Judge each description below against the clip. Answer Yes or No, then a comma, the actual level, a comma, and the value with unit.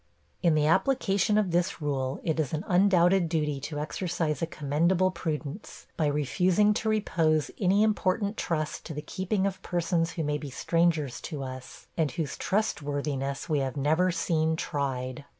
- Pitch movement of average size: Yes, average, 3.9 semitones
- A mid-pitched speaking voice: Yes, medium, 160 Hz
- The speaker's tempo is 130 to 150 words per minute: No, average, 165 wpm